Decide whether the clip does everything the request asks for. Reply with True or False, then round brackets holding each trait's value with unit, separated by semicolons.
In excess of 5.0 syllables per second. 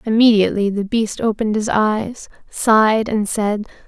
False (4.8 syllables/s)